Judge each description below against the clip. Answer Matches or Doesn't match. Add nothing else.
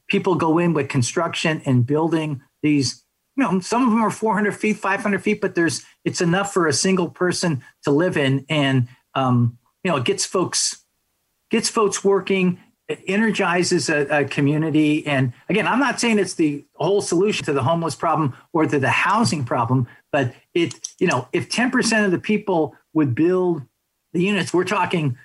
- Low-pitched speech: Doesn't match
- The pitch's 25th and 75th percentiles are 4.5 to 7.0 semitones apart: Matches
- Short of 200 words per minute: Matches